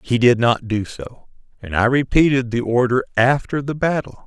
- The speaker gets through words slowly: No, average, 185 wpm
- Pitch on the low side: Yes, low, 125 Hz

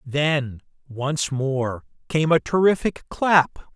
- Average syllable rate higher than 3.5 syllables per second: No, 3.1 syllables/s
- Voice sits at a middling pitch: Yes, medium, 145 Hz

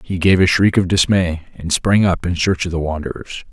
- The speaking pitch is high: No, very low, 90 Hz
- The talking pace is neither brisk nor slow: No, fast, 240 wpm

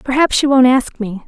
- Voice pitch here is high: Yes, very high, 255 Hz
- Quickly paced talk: Yes, fast, 235 wpm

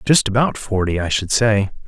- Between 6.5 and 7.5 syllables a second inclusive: No, 4.9 syllables/s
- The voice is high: No, low, 105 Hz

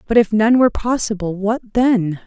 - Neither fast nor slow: Yes, average, 160 wpm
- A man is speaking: No, female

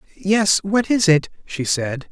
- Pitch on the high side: No, medium, 180 Hz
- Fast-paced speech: No, average, 170 wpm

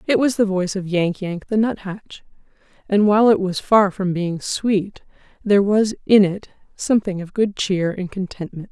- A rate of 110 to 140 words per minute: No, average, 185 wpm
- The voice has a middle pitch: No, high, 195 Hz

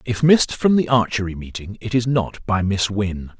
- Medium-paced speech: No, fast, 210 wpm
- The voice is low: Yes, low, 110 Hz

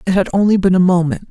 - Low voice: No, medium, 185 Hz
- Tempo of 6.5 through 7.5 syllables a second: Yes, 7.0 syllables/s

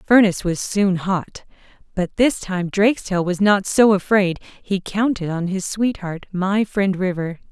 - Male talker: No, female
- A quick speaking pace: No, average, 170 wpm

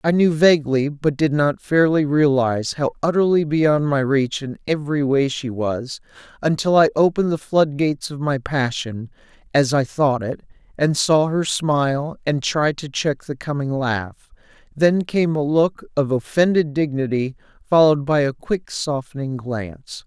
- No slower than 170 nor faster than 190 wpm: No, average, 160 wpm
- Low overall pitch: No, medium, 145 Hz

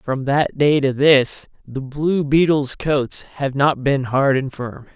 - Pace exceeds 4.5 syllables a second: No, 3.4 syllables/s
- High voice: No, medium, 140 Hz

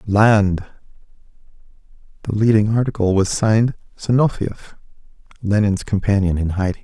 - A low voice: Yes, low, 105 Hz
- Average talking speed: No, slow, 90 wpm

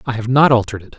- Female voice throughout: No, male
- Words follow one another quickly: Yes, fast, 305 wpm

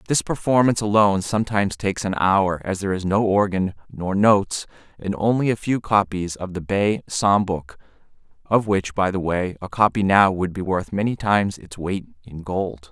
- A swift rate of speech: No, average, 190 wpm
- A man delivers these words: Yes, male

